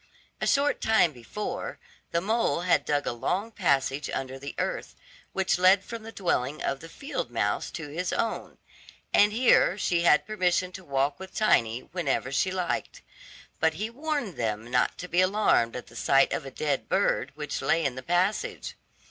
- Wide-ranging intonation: Yes, wide, 6.8 semitones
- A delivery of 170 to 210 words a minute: Yes, average, 180 wpm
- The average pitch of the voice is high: No, medium, 175 Hz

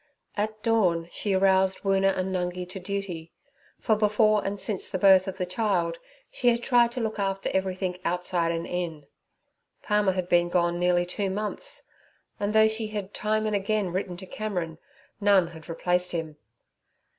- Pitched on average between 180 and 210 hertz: Yes, high, 190 Hz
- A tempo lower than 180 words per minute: Yes, average, 170 wpm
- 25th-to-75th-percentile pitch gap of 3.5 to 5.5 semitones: No, average, 2.9 semitones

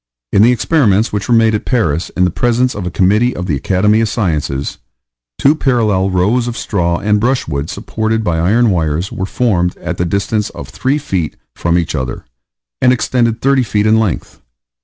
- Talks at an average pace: Yes, average, 190 wpm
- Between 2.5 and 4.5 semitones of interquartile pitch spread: No, average, 5.0 semitones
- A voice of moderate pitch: No, low, 105 Hz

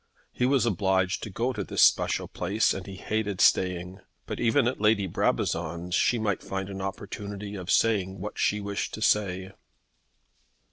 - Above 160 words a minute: Yes, average, 170 wpm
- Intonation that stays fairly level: Yes, narrow, 2.3 semitones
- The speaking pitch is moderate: No, low, 100 Hz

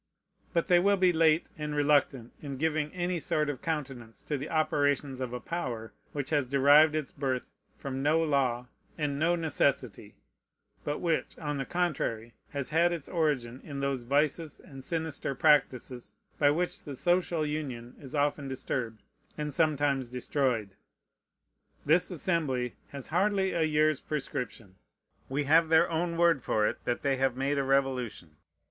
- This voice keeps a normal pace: Yes, average, 160 wpm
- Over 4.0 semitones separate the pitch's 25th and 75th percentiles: No, average, 3.4 semitones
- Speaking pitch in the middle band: Yes, medium, 145 Hz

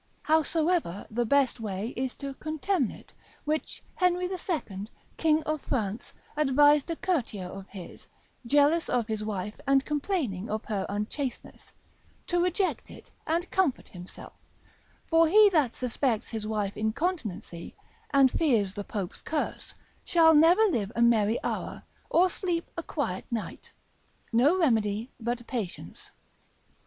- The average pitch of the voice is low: No, very high, 265 Hz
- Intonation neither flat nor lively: No, wide, 7.2 semitones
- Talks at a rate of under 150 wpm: Yes, slow, 135 wpm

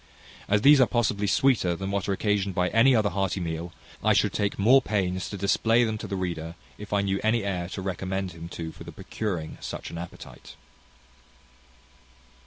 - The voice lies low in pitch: Yes, low, 100 Hz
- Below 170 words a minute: No, average, 195 wpm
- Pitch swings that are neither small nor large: Yes, average, 3.0 semitones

